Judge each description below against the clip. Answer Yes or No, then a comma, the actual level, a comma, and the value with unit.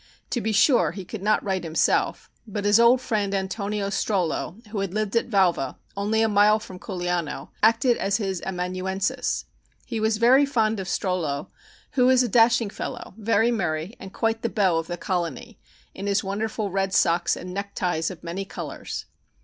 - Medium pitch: No, high, 200 Hz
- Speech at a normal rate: Yes, average, 180 wpm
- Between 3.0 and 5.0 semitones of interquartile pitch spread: Yes, average, 3.3 semitones